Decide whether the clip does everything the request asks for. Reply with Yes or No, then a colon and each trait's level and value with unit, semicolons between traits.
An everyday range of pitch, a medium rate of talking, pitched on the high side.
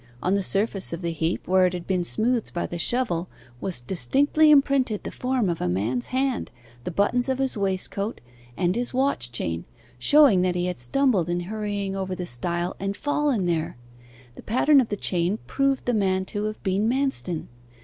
No: wide, 6.0 semitones; average, 190 wpm; high, 195 Hz